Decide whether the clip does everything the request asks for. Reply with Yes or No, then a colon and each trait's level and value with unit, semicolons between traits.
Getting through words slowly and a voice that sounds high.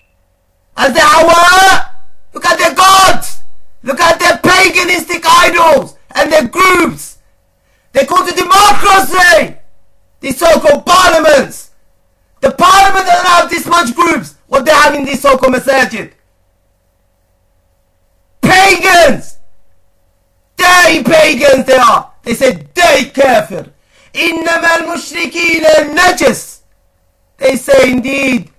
Yes: slow, 105 wpm; very high, 305 Hz